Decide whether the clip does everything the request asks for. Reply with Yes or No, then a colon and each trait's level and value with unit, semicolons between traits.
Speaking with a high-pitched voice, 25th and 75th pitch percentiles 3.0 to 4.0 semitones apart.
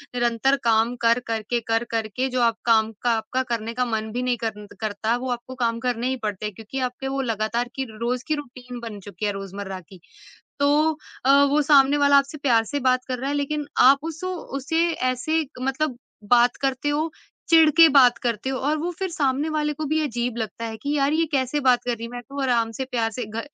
Yes: very high, 250 Hz; average, 3.5 semitones